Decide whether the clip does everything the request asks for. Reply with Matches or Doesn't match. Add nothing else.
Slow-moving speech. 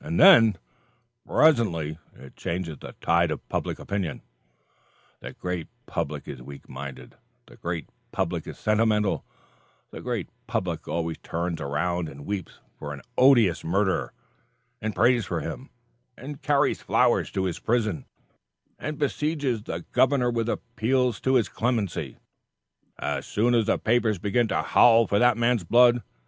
Doesn't match